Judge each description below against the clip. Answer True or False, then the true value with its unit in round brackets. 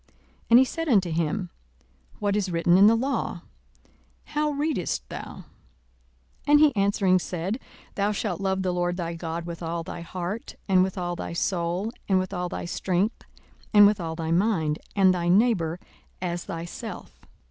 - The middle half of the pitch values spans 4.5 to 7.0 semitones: False (3.3 semitones)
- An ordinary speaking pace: True (170 wpm)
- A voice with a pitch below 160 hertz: False (185 Hz)